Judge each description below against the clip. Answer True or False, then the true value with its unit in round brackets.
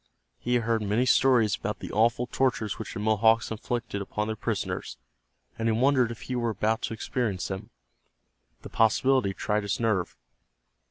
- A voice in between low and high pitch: False (110 Hz)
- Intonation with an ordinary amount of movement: False (2.3 semitones)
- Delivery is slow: False (170 wpm)